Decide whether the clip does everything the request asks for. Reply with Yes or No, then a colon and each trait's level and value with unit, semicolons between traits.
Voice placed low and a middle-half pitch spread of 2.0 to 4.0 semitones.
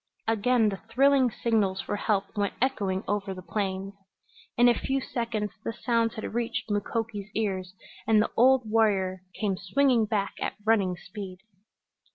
No: high, 215 Hz; average, 3.1 semitones